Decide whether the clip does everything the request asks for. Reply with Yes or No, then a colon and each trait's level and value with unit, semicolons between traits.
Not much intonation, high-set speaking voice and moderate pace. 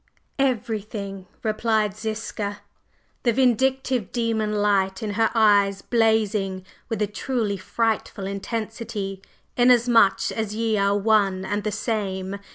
No: narrow, 2.2 semitones; high, 215 Hz; slow, 115 wpm